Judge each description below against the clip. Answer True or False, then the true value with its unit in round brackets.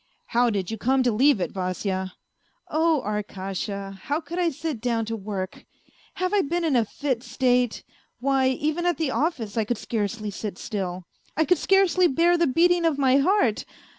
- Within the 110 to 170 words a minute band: False (195 wpm)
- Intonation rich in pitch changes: True (7.4 semitones)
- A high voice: True (255 Hz)